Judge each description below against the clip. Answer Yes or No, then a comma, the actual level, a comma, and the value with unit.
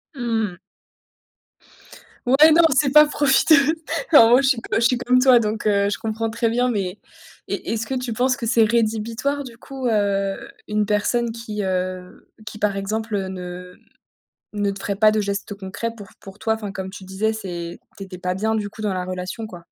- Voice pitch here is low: No, high, 215 Hz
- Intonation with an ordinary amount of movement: Yes, average, 3.1 semitones